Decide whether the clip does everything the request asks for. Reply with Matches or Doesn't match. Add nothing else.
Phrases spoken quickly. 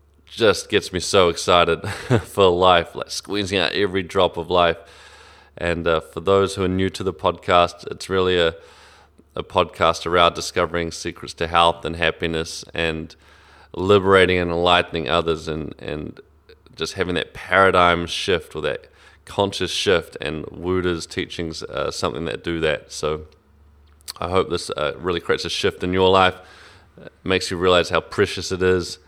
Doesn't match